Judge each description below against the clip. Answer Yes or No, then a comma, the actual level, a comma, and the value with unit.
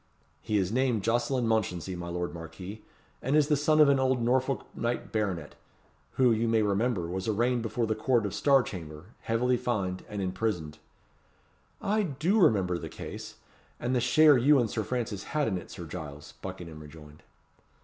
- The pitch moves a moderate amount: No, wide, 5.7 semitones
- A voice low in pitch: Yes, low, 110 Hz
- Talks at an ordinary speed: Yes, average, 180 wpm